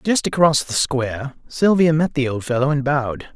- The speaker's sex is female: No, male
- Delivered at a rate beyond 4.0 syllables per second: Yes, 5.2 syllables/s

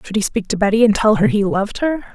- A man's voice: No, female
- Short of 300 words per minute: No, fast, 310 wpm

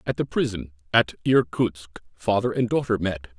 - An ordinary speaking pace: Yes, average, 160 wpm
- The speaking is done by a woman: No, male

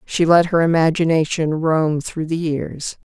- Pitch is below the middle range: No, medium, 160 Hz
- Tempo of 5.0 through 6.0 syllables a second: No, 4.1 syllables/s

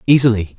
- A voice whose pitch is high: No, low, 110 Hz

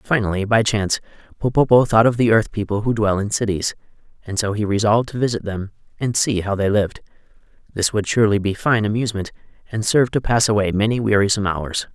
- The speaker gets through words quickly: No, average, 195 wpm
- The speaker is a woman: No, male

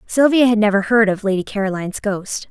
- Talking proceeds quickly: No, average, 190 wpm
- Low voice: No, high, 210 Hz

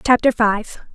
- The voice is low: No, high, 225 Hz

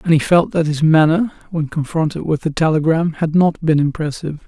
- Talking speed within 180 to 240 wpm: Yes, average, 200 wpm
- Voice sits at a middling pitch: Yes, medium, 160 Hz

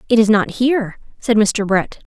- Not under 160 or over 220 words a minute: Yes, average, 200 wpm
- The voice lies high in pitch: Yes, high, 220 Hz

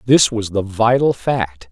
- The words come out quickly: No, average, 175 wpm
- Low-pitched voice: Yes, low, 110 Hz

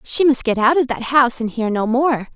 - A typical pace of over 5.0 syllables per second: Yes, 5.5 syllables/s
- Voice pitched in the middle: No, very high, 250 Hz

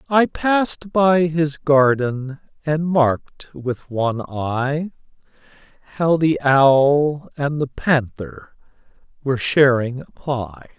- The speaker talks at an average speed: No, slow, 110 wpm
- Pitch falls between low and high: Yes, medium, 145 Hz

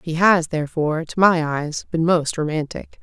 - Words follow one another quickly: No, average, 180 wpm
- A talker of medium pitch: Yes, medium, 160 Hz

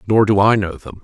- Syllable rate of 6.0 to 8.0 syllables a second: No, 5.8 syllables/s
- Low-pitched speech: Yes, low, 105 Hz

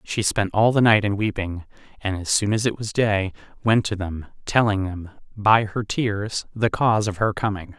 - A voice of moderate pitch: No, low, 105 Hz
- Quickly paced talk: Yes, fast, 210 wpm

